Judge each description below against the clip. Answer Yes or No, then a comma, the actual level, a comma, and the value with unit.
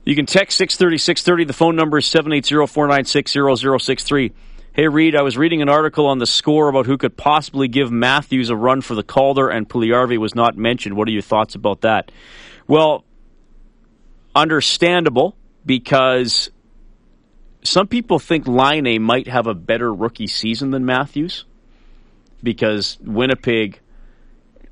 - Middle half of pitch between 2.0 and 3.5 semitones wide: No, average, 4.1 semitones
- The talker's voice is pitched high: No, low, 135 Hz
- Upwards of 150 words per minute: Yes, average, 170 wpm